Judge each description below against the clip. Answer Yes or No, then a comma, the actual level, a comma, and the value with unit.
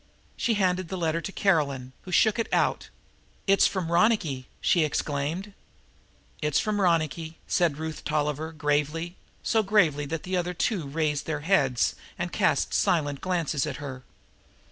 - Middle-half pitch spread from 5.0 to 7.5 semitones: No, average, 3.9 semitones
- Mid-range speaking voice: Yes, medium, 160 Hz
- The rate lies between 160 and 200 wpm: No, average, 150 wpm